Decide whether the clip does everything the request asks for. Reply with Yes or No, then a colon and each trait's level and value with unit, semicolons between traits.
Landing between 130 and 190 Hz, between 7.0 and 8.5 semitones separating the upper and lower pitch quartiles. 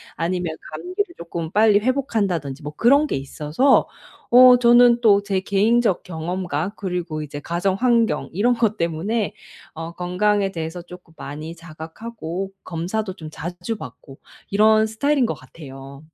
No: medium, 185 Hz; wide, 5.5 semitones